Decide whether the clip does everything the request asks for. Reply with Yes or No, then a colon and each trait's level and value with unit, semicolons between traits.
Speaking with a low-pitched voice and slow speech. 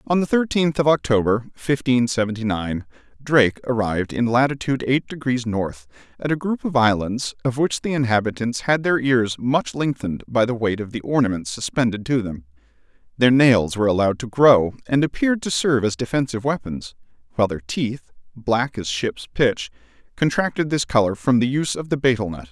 No: low, 125 Hz; average, 180 wpm